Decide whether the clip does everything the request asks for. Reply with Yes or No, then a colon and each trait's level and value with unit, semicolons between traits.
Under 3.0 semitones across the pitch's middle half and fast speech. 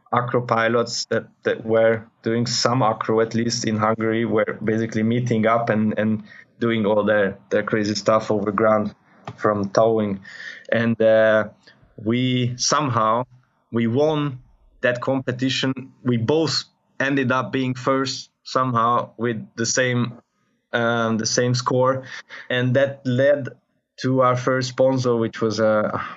No: narrow, 2.5 semitones; average, 140 wpm